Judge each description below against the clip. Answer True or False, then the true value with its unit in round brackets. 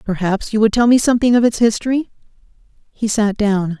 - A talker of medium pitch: False (220 Hz)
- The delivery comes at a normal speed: True (190 wpm)